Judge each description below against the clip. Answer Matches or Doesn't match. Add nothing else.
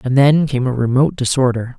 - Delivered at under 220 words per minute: Matches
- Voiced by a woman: Doesn't match